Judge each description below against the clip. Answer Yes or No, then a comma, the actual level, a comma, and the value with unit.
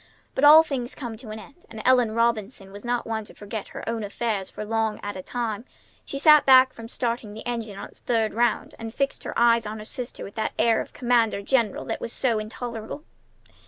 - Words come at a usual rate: No, fast, 225 wpm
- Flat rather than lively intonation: Yes, narrow, 2.3 semitones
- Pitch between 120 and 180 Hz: No, high, 230 Hz